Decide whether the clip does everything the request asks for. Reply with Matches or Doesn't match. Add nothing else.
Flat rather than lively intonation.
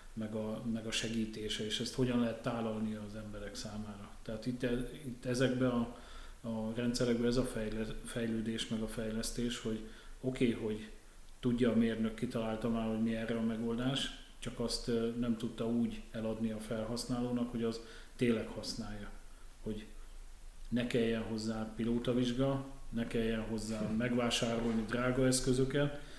Matches